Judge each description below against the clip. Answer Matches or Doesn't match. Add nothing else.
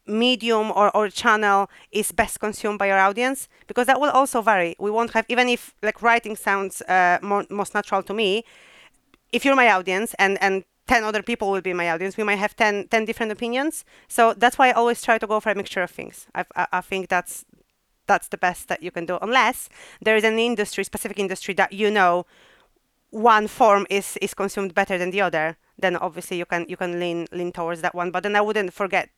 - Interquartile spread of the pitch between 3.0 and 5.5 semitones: Matches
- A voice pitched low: Doesn't match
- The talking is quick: Matches